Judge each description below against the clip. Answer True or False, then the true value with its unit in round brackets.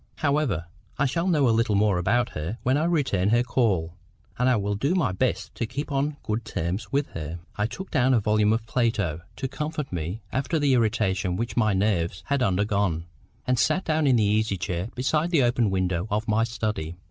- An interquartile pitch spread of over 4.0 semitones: True (5.6 semitones)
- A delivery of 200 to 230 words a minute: True (205 wpm)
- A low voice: True (110 Hz)